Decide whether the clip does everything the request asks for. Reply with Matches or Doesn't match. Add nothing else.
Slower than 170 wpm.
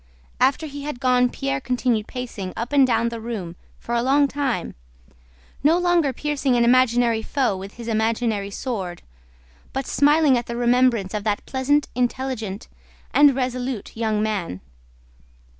Matches